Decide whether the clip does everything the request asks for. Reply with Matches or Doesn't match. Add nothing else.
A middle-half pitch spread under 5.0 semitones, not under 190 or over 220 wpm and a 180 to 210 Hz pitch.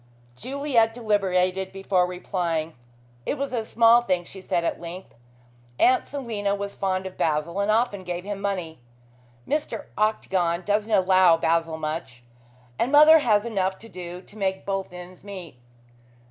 Doesn't match